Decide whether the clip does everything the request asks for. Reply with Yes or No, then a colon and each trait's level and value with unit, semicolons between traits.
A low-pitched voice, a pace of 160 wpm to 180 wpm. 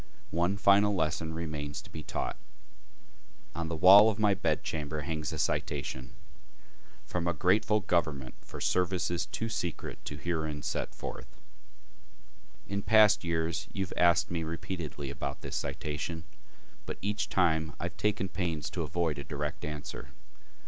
No: very low, 85 Hz; average, 150 wpm